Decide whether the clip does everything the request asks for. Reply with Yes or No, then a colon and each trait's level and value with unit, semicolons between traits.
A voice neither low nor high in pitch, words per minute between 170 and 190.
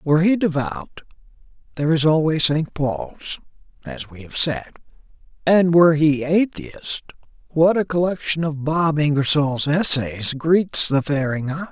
No: medium, 155 Hz; average, 140 wpm